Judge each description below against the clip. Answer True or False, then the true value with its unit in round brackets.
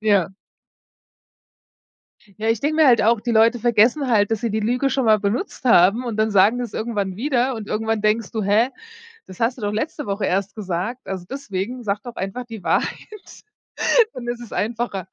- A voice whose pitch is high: True (225 Hz)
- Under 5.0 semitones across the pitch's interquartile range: True (3.0 semitones)